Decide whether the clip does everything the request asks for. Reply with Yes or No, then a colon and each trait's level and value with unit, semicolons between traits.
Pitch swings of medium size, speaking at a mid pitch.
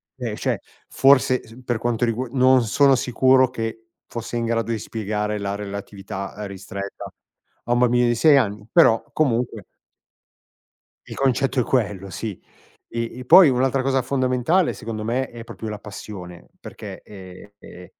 No: average, 3.6 semitones; low, 115 Hz